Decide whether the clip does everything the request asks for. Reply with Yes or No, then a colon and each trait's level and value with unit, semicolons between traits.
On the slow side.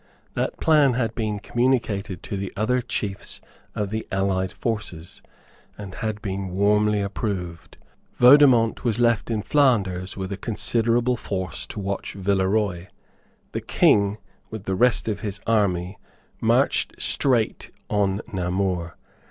Yes: slow, 130 wpm